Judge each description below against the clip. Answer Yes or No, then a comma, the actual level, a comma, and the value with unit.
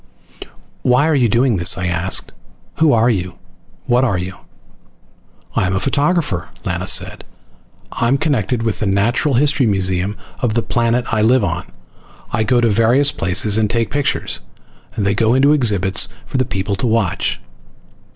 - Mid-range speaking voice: No, low, 115 Hz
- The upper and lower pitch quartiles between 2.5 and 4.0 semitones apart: No, average, 4.7 semitones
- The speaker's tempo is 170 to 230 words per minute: No, average, 160 wpm